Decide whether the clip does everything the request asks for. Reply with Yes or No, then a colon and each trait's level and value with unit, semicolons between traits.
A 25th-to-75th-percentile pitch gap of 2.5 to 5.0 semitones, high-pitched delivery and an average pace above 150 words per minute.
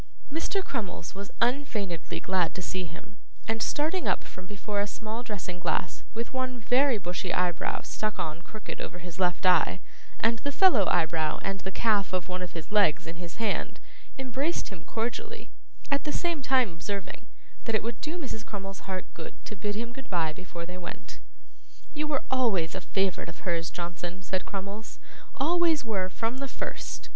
No: wide, 5.4 semitones; high, 205 Hz; average, 180 wpm